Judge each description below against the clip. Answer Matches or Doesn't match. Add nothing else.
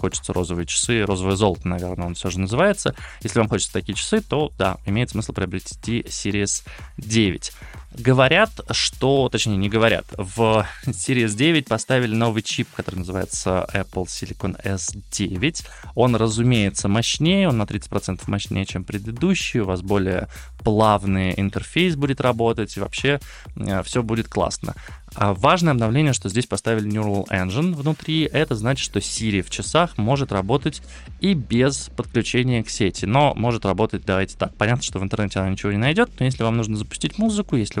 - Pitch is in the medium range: Doesn't match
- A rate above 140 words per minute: Matches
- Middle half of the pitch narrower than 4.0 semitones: Doesn't match